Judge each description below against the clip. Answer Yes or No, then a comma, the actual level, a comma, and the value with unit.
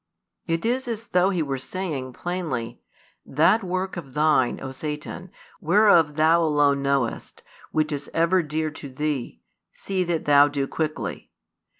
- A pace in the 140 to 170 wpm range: Yes, average, 155 wpm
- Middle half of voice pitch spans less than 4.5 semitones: Yes, average, 4.0 semitones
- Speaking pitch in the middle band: Yes, medium, 155 Hz